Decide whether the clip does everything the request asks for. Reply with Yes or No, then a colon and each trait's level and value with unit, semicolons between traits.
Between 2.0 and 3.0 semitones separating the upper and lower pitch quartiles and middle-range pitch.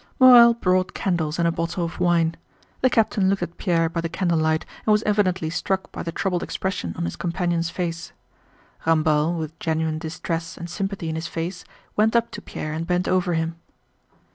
Yes: narrow, 2.5 semitones; medium, 170 Hz